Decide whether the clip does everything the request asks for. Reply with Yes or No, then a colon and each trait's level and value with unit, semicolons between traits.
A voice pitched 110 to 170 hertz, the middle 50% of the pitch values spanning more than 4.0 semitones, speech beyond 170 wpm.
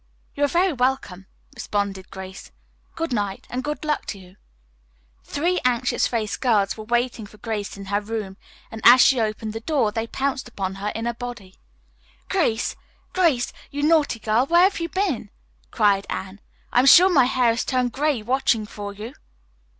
No: high, 235 Hz; average, 4.8 semitones; average, 180 wpm